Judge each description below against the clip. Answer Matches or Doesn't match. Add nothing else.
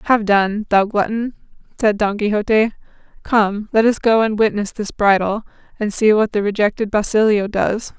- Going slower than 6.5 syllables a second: Matches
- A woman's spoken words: Matches